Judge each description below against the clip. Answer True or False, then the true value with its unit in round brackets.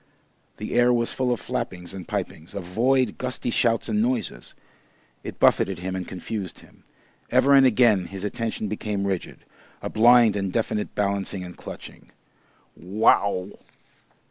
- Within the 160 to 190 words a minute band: False (145 wpm)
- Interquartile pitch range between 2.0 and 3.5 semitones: False (4.2 semitones)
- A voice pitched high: False (105 Hz)